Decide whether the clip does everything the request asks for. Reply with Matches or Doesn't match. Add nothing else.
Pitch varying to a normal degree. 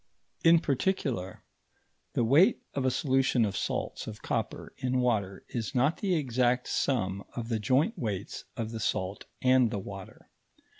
Matches